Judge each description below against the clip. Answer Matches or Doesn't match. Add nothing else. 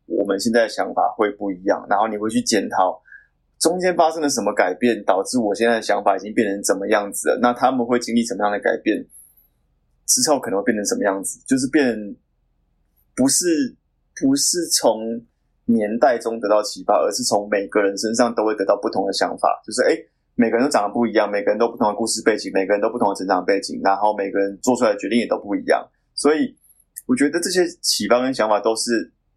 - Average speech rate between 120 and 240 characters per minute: Doesn't match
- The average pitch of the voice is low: Matches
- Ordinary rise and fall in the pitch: Matches